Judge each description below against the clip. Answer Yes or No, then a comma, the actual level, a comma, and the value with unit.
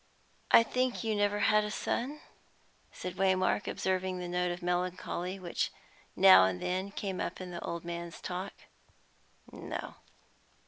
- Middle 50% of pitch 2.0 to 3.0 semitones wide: Yes, narrow, 2.4 semitones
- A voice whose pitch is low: No, medium, 185 Hz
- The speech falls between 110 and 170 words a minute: Yes, average, 150 wpm